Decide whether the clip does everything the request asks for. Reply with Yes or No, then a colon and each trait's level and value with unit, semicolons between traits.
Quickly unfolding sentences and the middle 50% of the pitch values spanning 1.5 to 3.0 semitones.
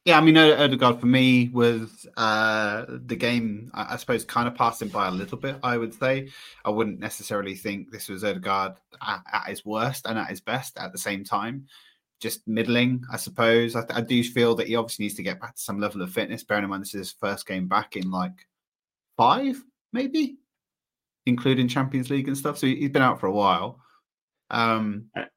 No: fast, 210 wpm; average, 4.1 semitones